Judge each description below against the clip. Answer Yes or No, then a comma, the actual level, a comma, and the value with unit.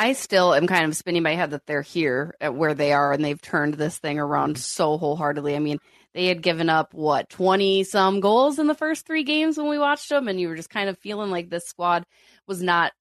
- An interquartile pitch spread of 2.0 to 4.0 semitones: No, average, 5.2 semitones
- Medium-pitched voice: Yes, medium, 175 Hz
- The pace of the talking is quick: Yes, fast, 250 wpm